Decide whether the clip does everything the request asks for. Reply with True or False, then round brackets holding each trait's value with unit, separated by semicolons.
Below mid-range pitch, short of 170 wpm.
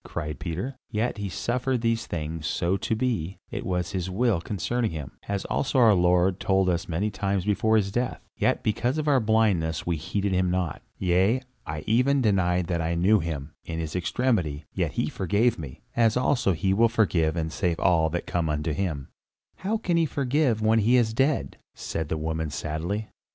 False (95 Hz; 195 wpm)